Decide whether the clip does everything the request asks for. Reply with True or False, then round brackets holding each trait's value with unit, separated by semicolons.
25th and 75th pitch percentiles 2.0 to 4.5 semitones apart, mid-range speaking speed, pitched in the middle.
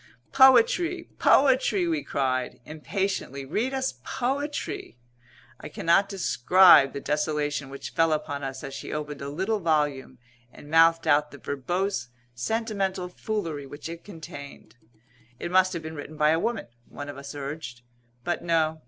False (5.3 semitones; 150 wpm; 160 Hz)